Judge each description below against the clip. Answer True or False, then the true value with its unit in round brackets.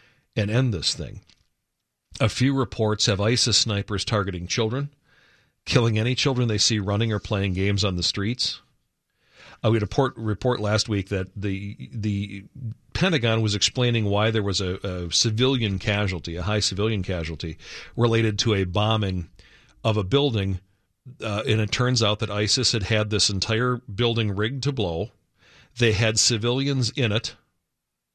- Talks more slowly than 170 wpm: True (160 wpm)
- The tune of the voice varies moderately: True (3.0 semitones)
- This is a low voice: True (110 Hz)